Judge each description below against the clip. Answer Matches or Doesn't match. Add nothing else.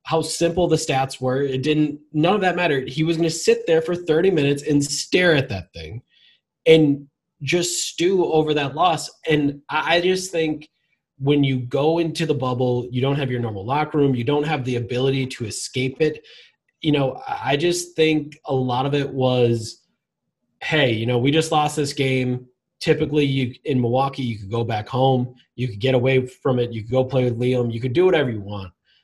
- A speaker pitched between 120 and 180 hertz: Matches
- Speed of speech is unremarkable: Doesn't match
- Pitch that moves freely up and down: Doesn't match